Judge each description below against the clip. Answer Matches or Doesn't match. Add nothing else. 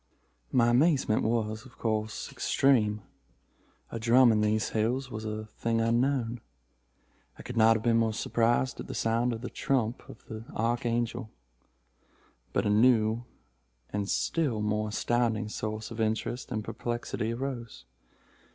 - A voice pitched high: Doesn't match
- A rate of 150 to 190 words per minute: Doesn't match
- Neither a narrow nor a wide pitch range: Doesn't match